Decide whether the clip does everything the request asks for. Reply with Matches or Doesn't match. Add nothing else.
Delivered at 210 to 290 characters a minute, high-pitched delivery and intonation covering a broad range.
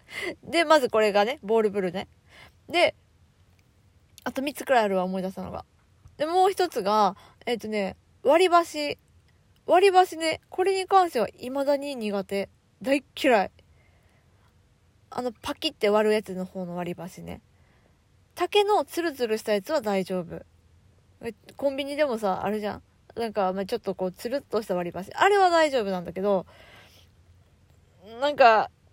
Matches